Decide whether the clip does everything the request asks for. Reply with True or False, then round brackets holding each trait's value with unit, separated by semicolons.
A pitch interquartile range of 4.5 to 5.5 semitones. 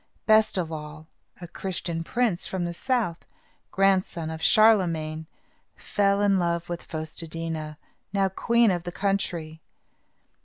False (3.5 semitones)